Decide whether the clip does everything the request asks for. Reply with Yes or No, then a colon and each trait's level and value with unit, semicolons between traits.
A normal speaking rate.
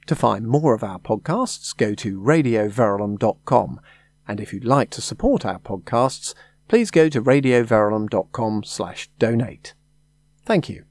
No: slow, 130 wpm